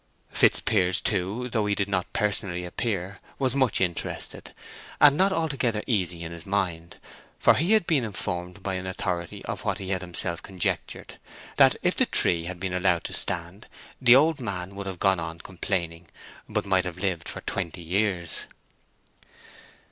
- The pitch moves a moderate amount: Yes, average, 3.3 semitones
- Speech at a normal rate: Yes, average, 170 wpm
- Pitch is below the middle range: Yes, very low, 95 Hz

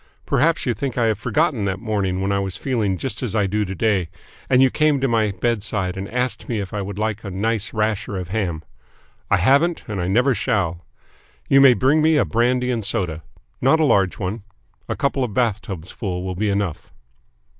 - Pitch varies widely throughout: No, average, 4.6 semitones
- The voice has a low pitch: Yes, low, 110 Hz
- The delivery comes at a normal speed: No, fast, 215 wpm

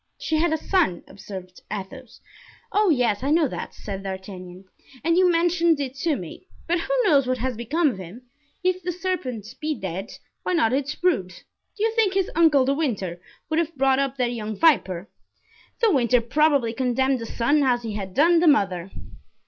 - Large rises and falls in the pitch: Yes, wide, 7.6 semitones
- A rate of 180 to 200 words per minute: Yes, average, 190 wpm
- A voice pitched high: Yes, very high, 265 Hz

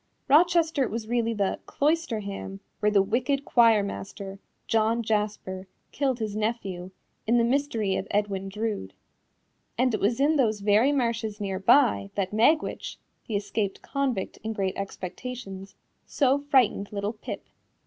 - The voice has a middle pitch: No, high, 220 Hz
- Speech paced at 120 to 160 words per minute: Yes, average, 140 wpm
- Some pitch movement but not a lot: Yes, average, 4.0 semitones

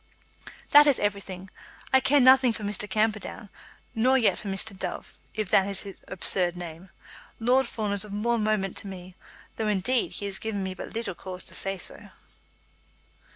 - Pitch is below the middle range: No, high, 205 Hz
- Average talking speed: Yes, average, 180 wpm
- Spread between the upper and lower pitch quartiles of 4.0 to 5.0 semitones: No, average, 3.0 semitones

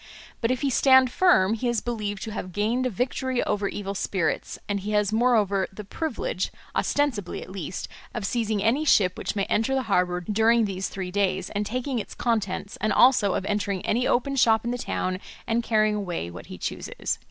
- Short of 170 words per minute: No, average, 200 wpm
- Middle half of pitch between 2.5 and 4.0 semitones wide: Yes, average, 3.6 semitones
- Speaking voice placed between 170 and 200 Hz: No, high, 215 Hz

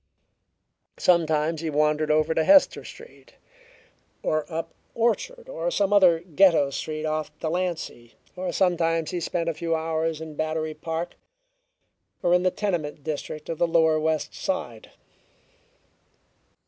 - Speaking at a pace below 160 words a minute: Yes, slow, 135 wpm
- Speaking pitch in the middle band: Yes, medium, 160 Hz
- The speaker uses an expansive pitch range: No, narrow, 2.4 semitones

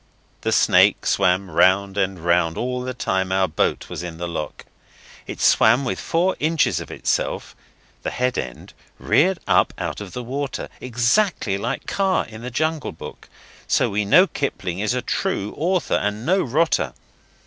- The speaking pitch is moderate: No, low, 115 Hz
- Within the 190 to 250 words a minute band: No, average, 170 wpm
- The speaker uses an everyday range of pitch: No, wide, 7.4 semitones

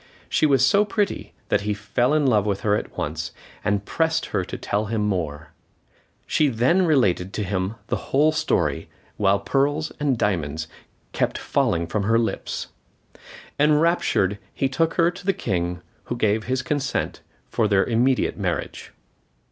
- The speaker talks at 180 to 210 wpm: No, average, 160 wpm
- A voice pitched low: Yes, low, 110 Hz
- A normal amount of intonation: No, wide, 6.8 semitones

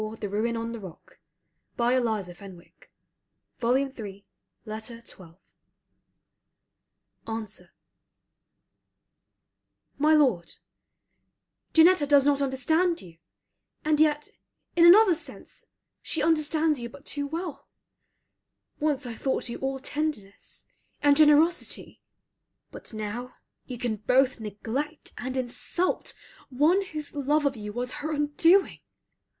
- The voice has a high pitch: Yes, very high, 270 Hz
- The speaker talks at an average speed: No, slow, 110 wpm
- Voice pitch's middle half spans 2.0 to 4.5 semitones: No, average, 5.1 semitones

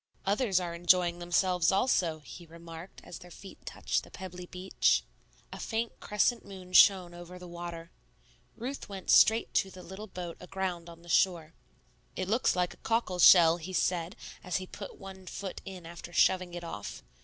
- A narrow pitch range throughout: Yes, narrow, 1.9 semitones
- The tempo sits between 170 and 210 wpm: Yes, average, 180 wpm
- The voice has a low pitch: No, medium, 180 Hz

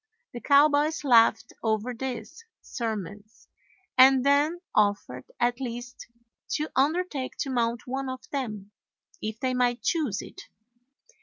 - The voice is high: Yes, very high, 250 Hz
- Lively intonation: No, average, 3.7 semitones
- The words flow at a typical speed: No, slow, 125 wpm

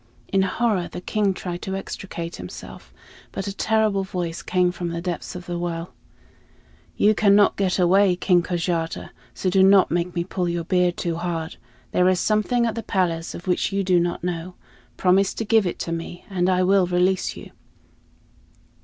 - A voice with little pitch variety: Yes, narrow, 2.0 semitones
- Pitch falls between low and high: Yes, medium, 180 Hz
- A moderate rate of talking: Yes, average, 185 wpm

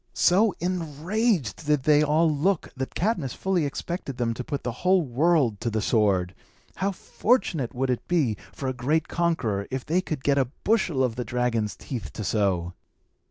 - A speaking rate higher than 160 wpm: Yes, average, 180 wpm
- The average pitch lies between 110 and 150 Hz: Yes, medium, 140 Hz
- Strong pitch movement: Yes, wide, 6.3 semitones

